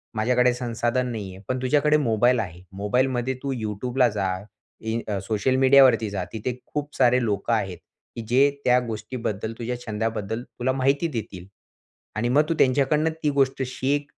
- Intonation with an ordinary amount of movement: Yes, average, 3.2 semitones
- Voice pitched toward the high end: No, low, 120 Hz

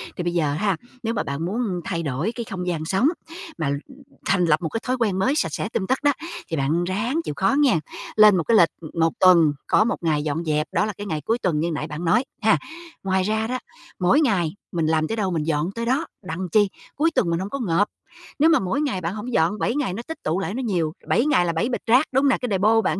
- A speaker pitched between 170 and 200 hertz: Yes, high, 190 Hz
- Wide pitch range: Yes, wide, 5.9 semitones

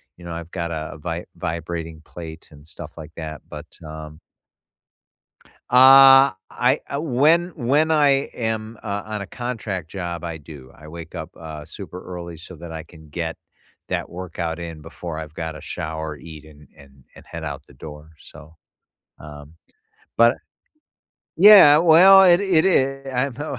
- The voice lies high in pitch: No, very low, 85 Hz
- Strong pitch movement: Yes, wide, 8.0 semitones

